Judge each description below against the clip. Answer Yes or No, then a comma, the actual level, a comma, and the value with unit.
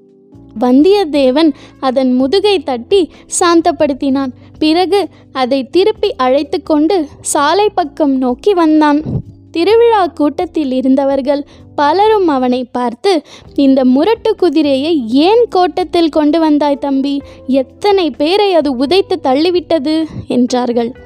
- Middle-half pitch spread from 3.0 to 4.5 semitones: No, average, 5.1 semitones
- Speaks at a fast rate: No, average, 95 wpm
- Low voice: No, very high, 305 Hz